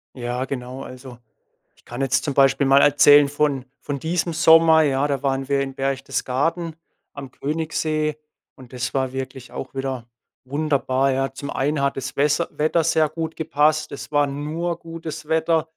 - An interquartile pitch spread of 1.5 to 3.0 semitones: Yes, narrow, 2.6 semitones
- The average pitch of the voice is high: No, medium, 140 Hz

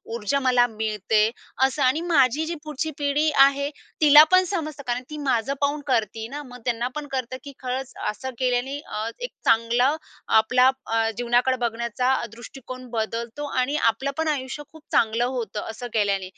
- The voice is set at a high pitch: Yes, very high, 255 Hz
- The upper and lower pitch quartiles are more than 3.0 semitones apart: Yes, average, 3.7 semitones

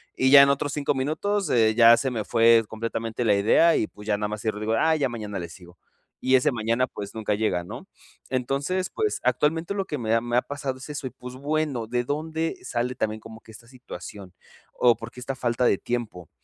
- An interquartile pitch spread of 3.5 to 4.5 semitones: Yes, average, 4.1 semitones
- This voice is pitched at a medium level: No, low, 120 Hz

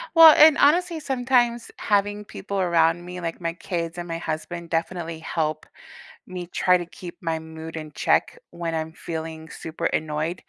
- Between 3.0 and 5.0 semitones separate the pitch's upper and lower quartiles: Yes, average, 3.5 semitones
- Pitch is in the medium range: Yes, medium, 170 Hz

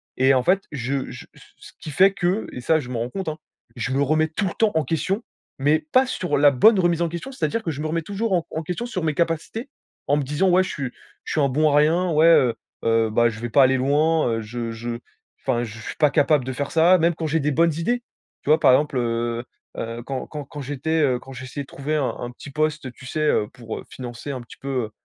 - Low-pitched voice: No, medium, 145 Hz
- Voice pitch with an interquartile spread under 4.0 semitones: No, average, 4.5 semitones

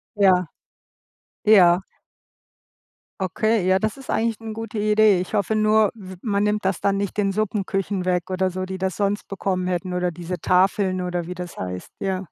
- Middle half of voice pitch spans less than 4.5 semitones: Yes, narrow, 2.5 semitones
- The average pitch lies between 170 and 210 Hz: Yes, high, 190 Hz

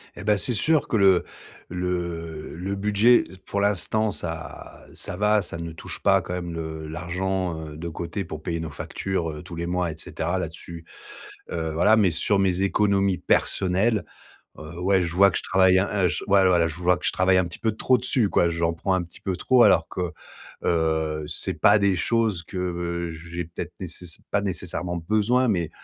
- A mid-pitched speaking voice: No, very low, 90 Hz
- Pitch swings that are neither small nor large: Yes, average, 3.0 semitones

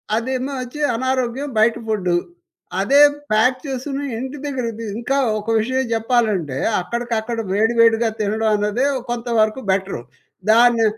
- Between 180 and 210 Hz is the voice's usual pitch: No, high, 235 Hz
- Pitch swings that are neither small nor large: Yes, average, 3.0 semitones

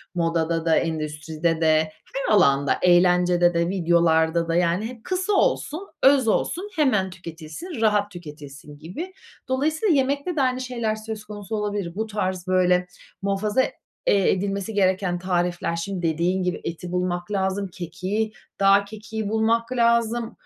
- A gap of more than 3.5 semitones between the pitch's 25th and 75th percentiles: Yes, average, 4.4 semitones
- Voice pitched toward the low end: No, high, 190 Hz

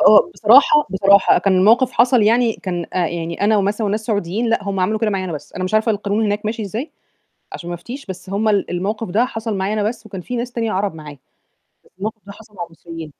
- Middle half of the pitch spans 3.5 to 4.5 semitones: No, average, 3.0 semitones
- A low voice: No, high, 205 Hz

